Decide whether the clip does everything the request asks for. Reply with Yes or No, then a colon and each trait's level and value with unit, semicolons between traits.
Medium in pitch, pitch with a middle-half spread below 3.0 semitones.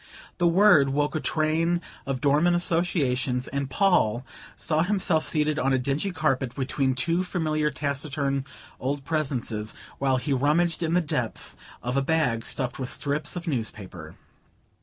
No: medium, 145 Hz; average, 3.8 semitones